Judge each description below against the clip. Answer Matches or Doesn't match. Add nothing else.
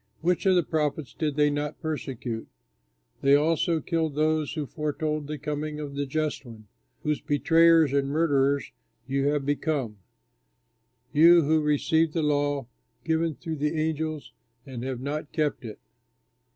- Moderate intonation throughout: Doesn't match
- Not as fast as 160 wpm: Matches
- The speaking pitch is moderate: Matches